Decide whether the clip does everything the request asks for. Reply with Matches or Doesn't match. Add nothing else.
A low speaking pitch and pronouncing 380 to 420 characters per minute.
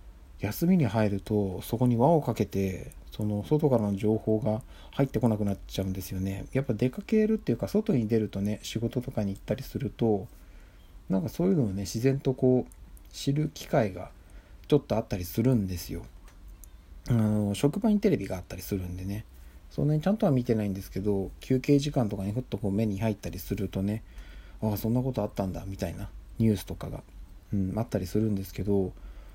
Matches